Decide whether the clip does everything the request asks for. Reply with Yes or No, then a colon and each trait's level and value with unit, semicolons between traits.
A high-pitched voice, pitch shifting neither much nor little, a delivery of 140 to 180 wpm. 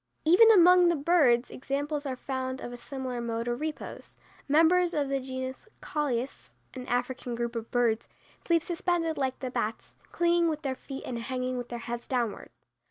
Yes: very high, 260 Hz; average, 4.5 semitones; average, 175 wpm